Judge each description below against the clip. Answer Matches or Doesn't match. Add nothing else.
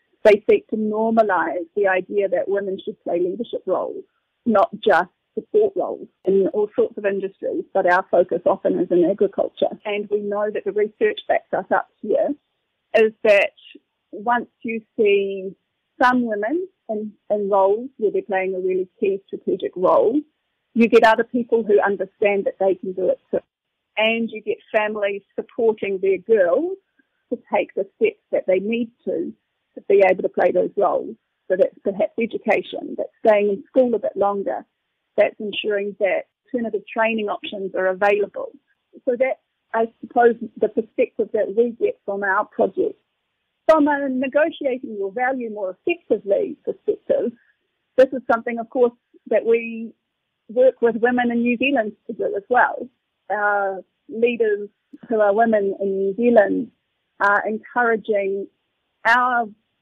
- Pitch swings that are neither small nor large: Doesn't match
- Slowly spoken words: Doesn't match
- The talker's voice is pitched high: Matches